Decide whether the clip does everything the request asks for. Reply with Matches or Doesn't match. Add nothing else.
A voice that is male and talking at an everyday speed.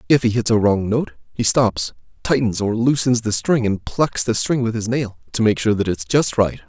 Doesn't match